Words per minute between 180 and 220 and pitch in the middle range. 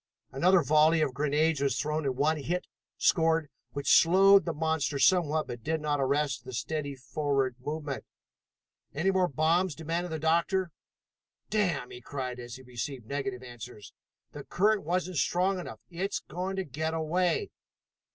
No: average, 155 wpm; medium, 155 Hz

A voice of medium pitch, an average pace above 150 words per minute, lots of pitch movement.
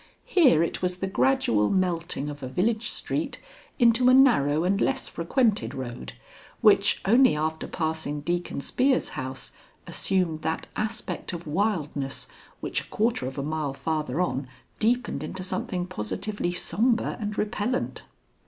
No: medium, 180 Hz; average, 145 wpm; wide, 6.6 semitones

